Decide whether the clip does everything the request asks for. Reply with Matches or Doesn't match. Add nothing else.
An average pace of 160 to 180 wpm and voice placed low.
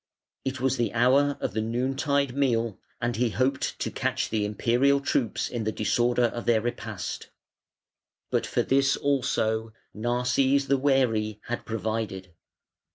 Doesn't match